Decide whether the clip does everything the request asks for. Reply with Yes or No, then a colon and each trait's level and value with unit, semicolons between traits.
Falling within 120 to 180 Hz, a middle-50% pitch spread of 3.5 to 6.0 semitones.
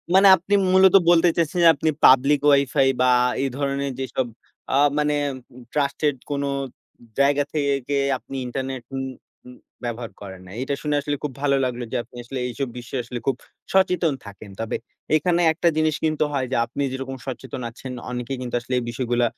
No: low, 135 Hz; average, 2.9 semitones